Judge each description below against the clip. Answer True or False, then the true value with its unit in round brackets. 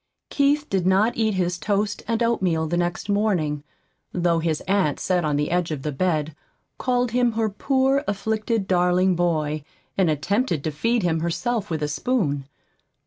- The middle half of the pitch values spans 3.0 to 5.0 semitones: False (5.5 semitones)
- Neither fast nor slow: True (170 wpm)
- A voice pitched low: False (185 Hz)